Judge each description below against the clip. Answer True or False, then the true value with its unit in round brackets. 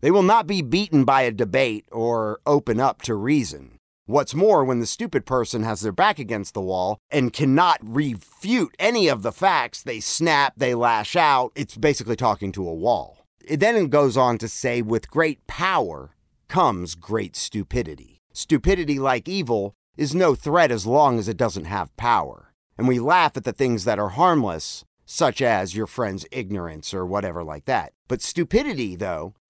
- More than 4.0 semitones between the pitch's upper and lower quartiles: True (5.4 semitones)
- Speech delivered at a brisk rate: False (185 wpm)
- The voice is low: True (125 Hz)